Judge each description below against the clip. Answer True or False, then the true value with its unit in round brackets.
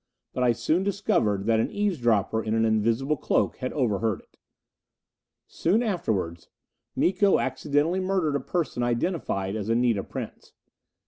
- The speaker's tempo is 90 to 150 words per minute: True (135 wpm)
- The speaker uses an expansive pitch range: True (7.9 semitones)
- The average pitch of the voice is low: True (125 Hz)